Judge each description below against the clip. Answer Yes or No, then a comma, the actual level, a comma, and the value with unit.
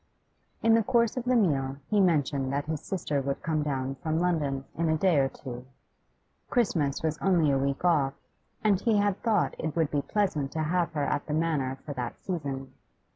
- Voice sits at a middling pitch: Yes, medium, 155 Hz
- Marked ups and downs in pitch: No, average, 4.8 semitones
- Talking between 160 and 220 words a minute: Yes, average, 200 wpm